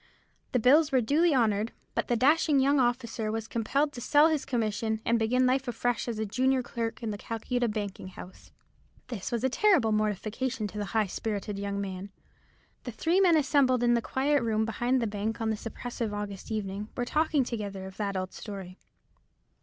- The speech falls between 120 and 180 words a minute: No, average, 195 wpm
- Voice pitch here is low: No, high, 230 Hz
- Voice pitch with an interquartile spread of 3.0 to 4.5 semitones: Yes, average, 3.6 semitones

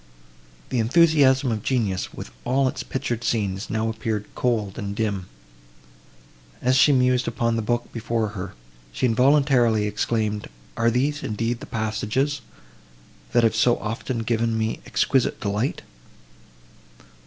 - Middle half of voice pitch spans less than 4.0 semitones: Yes, average, 2.7 semitones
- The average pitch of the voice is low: Yes, low, 115 Hz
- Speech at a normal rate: No, slow, 130 wpm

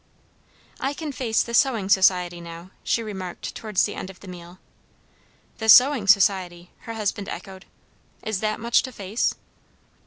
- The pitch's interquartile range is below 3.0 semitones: No, average, 3.7 semitones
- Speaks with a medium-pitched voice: No, high, 200 Hz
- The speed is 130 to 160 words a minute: Yes, average, 155 wpm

